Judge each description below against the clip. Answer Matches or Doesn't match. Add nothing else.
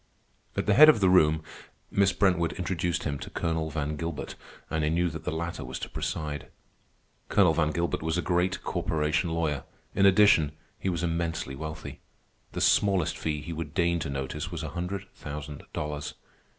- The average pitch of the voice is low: Matches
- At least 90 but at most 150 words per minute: Doesn't match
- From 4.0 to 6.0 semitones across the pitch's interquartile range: Doesn't match